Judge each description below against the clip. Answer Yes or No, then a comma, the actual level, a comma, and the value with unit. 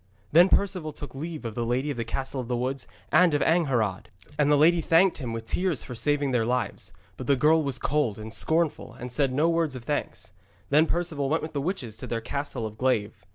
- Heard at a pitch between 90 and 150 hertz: Yes, medium, 140 Hz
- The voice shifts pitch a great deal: No, average, 4.6 semitones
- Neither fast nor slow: No, fast, 225 wpm